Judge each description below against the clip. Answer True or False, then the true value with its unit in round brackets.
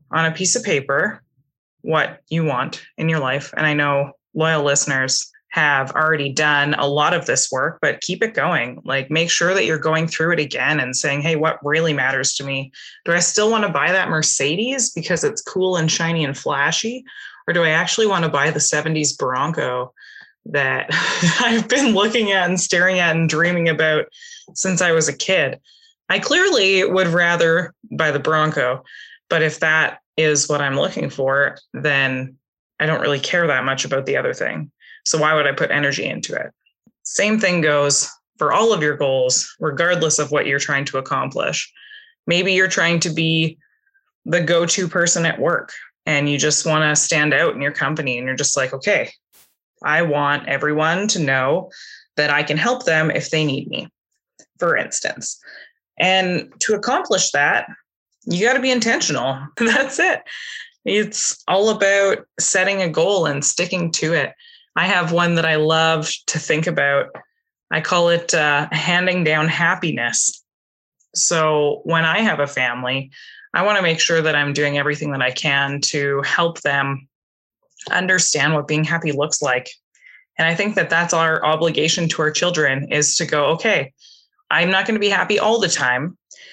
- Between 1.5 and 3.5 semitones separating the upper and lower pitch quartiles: False (4.2 semitones)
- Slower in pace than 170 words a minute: False (185 wpm)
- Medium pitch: True (160 Hz)